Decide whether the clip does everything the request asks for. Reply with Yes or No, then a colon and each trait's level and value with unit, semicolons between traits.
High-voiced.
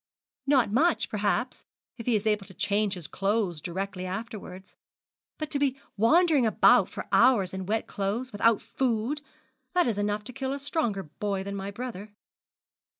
Yes: high, 210 Hz